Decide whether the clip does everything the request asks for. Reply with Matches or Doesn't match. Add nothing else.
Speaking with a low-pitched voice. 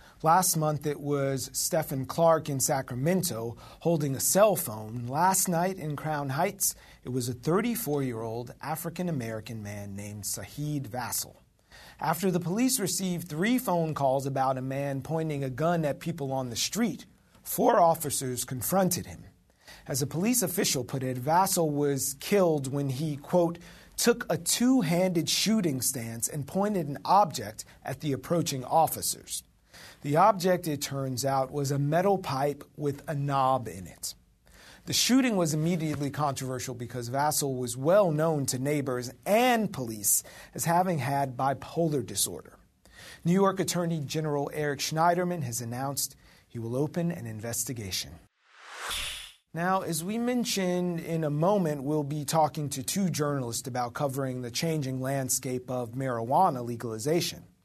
Doesn't match